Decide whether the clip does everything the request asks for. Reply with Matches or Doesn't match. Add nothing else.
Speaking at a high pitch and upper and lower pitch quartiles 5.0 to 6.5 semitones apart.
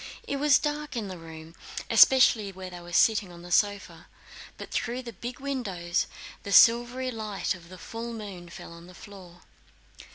Matches